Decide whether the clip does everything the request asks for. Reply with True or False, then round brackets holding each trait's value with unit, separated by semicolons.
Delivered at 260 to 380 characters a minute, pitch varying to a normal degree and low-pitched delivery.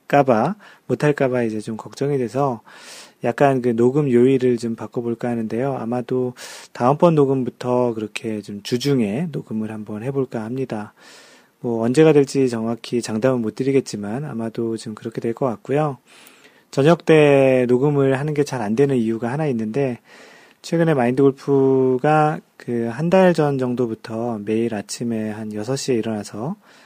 True (315 characters per minute; 3.4 semitones; 125 Hz)